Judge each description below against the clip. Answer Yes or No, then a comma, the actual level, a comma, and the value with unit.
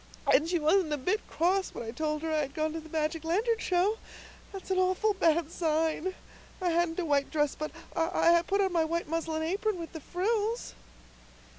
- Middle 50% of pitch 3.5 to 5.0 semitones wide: No, average, 3.1 semitones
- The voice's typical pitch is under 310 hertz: No, very high, 335 Hz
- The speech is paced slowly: No, average, 200 wpm